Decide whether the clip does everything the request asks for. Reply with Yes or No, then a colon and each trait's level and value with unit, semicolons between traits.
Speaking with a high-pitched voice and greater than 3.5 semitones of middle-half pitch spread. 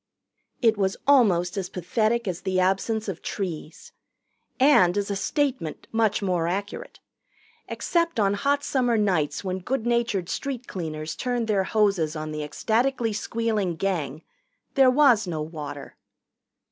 Yes: high, 200 Hz; average, 5.1 semitones